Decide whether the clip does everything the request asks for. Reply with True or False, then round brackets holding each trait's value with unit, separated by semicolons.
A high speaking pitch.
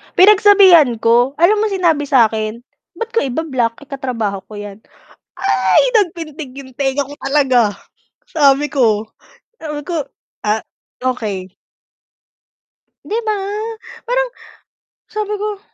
True (280 Hz)